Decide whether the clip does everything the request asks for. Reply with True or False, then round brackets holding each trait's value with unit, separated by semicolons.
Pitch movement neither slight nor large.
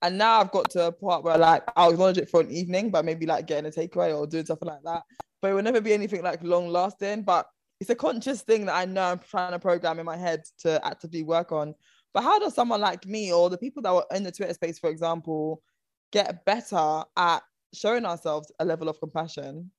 True (3.2 semitones)